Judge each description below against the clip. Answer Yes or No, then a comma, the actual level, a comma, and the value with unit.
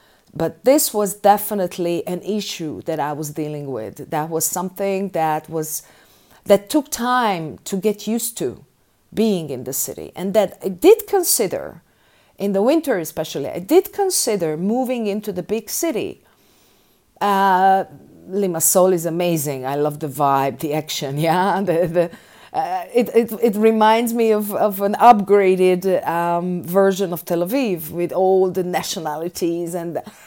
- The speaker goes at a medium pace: Yes, average, 155 wpm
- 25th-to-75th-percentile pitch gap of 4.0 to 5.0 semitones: Yes, average, 4.5 semitones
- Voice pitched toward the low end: No, high, 190 Hz